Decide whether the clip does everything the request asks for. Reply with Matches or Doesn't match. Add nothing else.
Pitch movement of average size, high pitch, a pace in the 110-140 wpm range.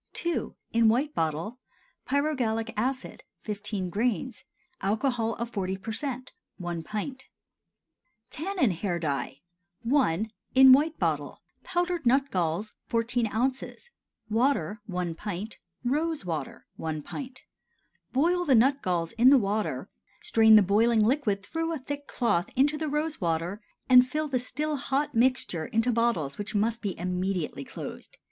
Doesn't match